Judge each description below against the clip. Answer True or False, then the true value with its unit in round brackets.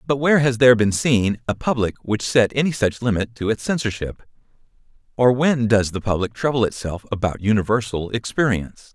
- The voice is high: False (115 Hz)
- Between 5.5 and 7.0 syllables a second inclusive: True (5.6 syllables/s)